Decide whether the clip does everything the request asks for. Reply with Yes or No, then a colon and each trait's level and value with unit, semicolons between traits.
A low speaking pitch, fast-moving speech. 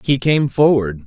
No: low, 125 Hz; average, 170 wpm